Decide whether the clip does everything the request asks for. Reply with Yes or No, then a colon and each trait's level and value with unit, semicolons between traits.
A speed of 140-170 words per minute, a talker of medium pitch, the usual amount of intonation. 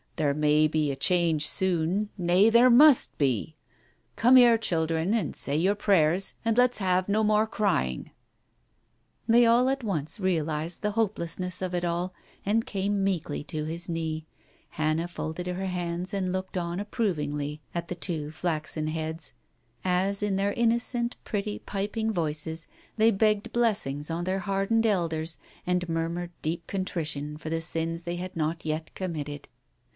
Yes: average, 155 wpm; medium, 175 Hz; average, 4.2 semitones